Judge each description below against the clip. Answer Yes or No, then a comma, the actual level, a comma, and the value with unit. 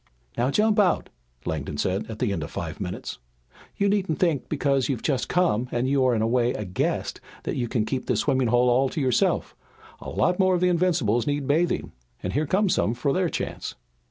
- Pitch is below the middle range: Yes, low, 130 Hz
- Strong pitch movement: Yes, wide, 6.6 semitones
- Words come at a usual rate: No, fast, 215 wpm